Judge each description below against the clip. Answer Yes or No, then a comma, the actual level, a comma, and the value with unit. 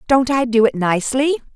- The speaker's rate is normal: Yes, average, 195 wpm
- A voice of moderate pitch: No, very high, 250 Hz